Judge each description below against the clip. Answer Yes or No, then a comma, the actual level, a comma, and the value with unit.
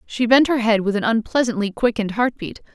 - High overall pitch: Yes, high, 225 Hz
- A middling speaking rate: No, fast, 220 wpm